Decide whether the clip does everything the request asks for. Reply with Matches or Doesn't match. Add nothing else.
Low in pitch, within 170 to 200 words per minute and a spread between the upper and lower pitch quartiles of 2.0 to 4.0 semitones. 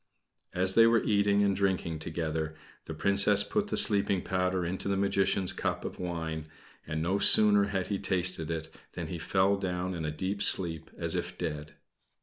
Matches